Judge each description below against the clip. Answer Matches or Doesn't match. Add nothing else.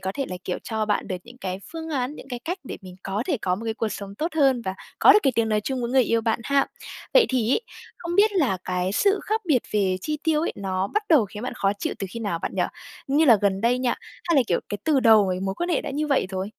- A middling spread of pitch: Doesn't match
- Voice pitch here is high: Matches